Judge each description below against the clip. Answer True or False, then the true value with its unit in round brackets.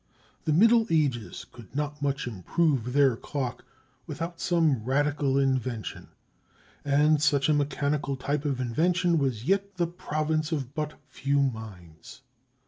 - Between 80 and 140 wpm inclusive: True (135 wpm)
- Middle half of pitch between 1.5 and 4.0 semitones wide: True (3.1 semitones)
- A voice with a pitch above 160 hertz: False (145 Hz)